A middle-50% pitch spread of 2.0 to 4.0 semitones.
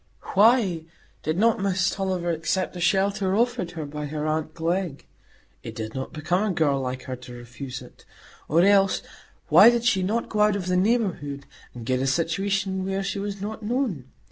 No: average, 5.0 semitones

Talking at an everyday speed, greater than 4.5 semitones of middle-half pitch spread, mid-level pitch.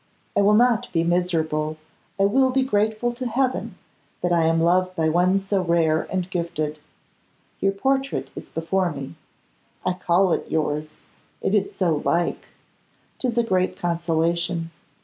No: average, 150 wpm; average, 3.8 semitones; medium, 180 Hz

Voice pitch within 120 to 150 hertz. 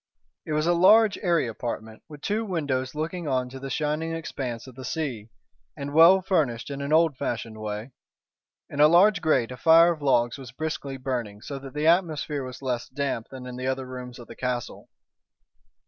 Yes: medium, 140 Hz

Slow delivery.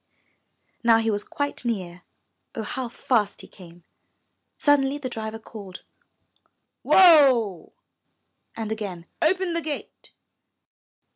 Yes: slow, 110 wpm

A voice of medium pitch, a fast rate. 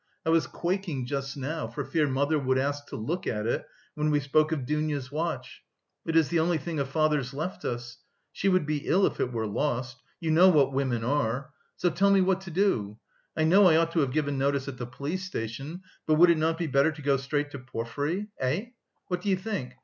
Yes: medium, 150 Hz; fast, 230 wpm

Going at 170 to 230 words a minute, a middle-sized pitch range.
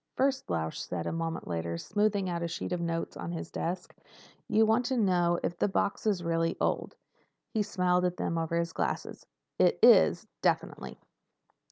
Yes: average, 175 wpm; average, 3.3 semitones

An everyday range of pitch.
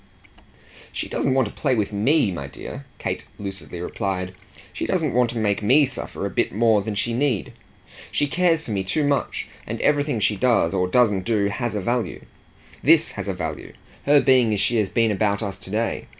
Yes: average, 4.6 semitones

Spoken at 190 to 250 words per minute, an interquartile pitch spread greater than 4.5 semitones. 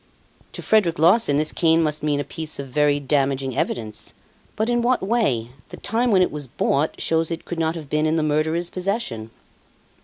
No: average, 195 wpm; average, 3.9 semitones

